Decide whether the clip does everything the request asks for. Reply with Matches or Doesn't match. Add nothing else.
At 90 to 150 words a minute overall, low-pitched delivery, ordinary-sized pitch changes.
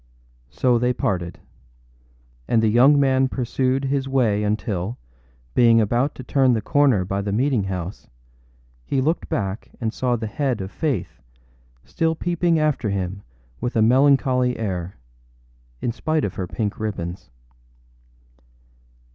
Matches